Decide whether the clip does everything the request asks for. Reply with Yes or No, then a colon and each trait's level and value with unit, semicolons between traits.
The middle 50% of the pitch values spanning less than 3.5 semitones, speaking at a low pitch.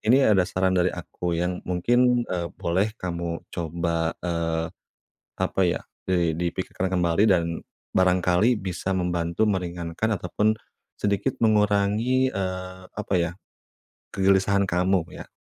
Yes: average, 2.7 semitones; very low, 90 Hz